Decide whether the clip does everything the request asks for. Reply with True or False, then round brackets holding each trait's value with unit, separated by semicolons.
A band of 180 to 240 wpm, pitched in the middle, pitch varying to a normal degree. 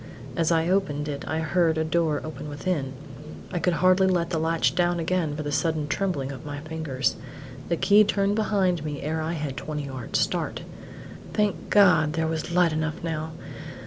True (185 wpm; 160 Hz; 3.1 semitones)